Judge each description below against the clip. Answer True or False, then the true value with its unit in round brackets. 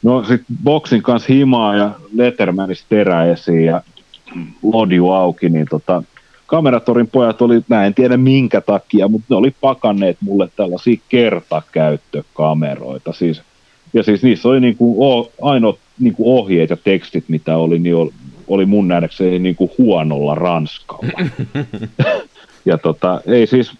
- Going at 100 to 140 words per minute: True (135 wpm)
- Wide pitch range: True (6.2 semitones)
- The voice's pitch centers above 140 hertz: False (105 Hz)